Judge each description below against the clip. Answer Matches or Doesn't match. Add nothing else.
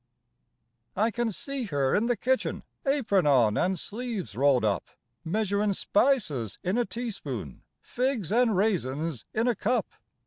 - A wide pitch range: Matches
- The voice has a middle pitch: Doesn't match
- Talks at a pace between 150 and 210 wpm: Doesn't match